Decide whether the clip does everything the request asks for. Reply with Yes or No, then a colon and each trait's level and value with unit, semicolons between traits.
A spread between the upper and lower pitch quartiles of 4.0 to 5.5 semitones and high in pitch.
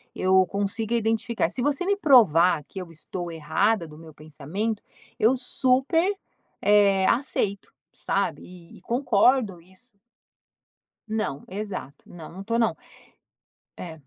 Yes: average, 5.2 semitones; high, 200 Hz